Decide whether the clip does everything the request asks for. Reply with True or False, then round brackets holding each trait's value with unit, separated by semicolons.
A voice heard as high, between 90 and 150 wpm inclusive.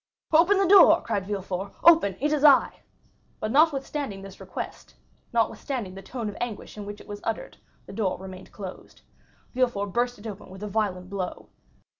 False (210 Hz; 175 wpm)